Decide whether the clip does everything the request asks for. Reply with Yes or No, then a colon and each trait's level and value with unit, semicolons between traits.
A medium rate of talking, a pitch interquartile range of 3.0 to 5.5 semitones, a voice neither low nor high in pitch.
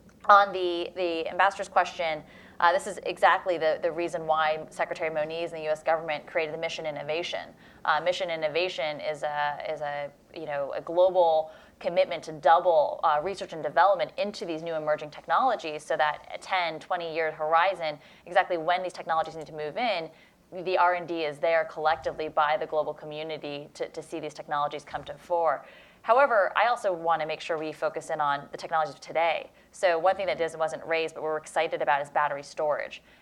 No: average, 190 wpm; narrow, 2.4 semitones; medium, 160 Hz